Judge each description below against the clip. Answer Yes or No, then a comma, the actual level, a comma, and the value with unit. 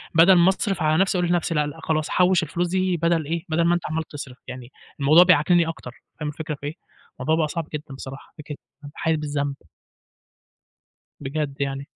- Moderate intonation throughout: Yes, average, 3.0 semitones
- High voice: No, medium, 155 Hz